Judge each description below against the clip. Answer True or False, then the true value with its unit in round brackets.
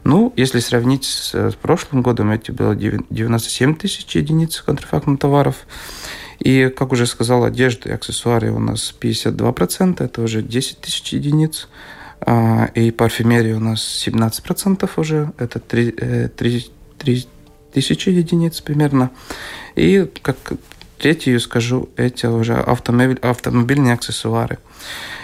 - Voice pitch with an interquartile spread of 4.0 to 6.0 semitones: False (3.6 semitones)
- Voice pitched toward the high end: False (125 Hz)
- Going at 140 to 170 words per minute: False (115 wpm)